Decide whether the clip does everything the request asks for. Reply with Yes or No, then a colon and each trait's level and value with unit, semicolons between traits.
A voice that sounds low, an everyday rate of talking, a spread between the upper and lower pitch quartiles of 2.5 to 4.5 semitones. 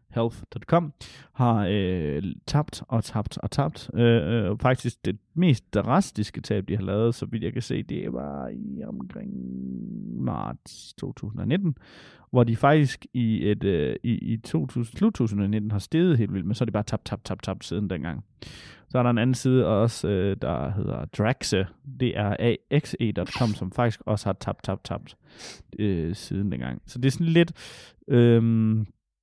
Yes: low, 115 Hz; average, 170 wpm; average, 4.0 semitones